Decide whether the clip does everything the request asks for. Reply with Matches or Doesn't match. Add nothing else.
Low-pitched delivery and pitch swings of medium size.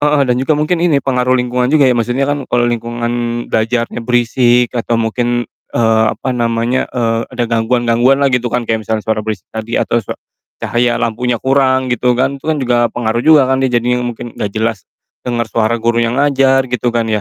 Doesn't match